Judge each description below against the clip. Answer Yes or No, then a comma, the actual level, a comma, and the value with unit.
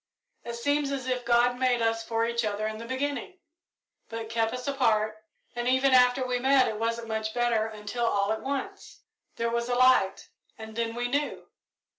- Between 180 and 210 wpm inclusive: Yes, average, 190 wpm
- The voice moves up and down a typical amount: No, narrow, 2.2 semitones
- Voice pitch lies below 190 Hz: No, high, 235 Hz